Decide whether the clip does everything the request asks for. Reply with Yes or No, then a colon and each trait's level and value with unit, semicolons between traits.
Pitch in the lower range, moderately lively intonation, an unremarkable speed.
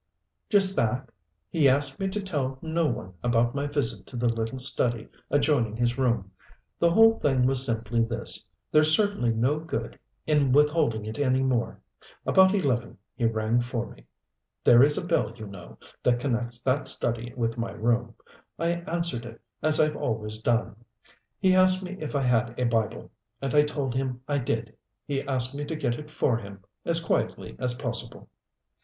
Yes: low, 130 Hz; average, 4.2 semitones; average, 180 wpm